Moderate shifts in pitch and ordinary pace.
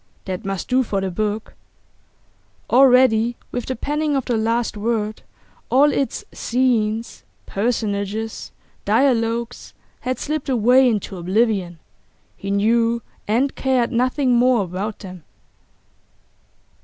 No: average, 3.3 semitones; slow, 115 wpm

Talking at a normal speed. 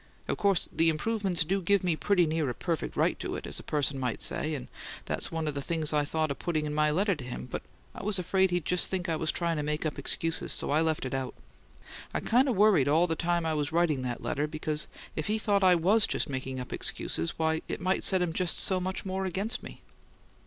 No: fast, 250 wpm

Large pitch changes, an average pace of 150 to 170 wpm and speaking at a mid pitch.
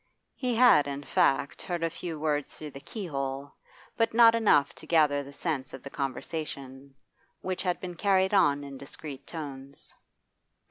No: average, 4.5 semitones; average, 165 wpm; medium, 150 Hz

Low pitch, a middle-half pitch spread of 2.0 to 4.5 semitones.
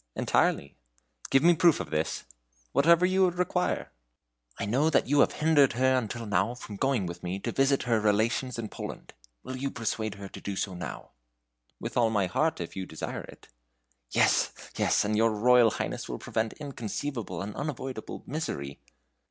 No: low, 120 Hz; wide, 5.4 semitones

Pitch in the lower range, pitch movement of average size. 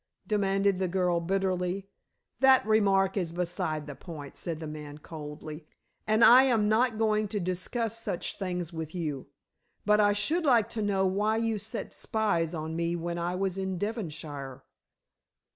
No: high, 190 Hz; average, 4.2 semitones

